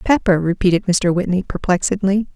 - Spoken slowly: Yes, slow, 125 wpm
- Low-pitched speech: No, medium, 185 Hz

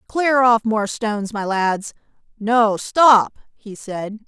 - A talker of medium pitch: No, high, 220 Hz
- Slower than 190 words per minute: Yes, average, 140 wpm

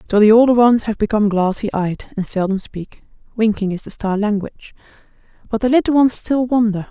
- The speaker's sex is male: No, female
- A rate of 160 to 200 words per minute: Yes, average, 190 wpm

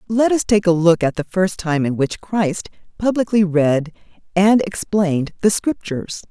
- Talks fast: No, average, 170 wpm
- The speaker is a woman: Yes, female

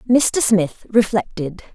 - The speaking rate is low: Yes, slow, 105 wpm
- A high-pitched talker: Yes, high, 210 Hz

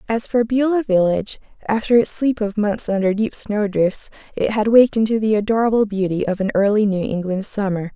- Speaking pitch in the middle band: No, high, 210 Hz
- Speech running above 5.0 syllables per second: Yes, 5.5 syllables/s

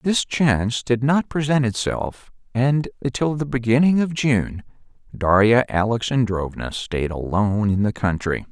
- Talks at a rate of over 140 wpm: No, slow, 135 wpm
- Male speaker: Yes, male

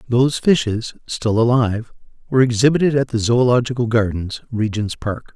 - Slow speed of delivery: Yes, slow, 110 wpm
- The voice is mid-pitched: No, low, 120 Hz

